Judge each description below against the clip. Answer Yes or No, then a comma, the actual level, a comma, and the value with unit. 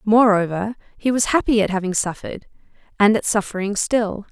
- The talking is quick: No, average, 155 wpm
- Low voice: No, high, 210 Hz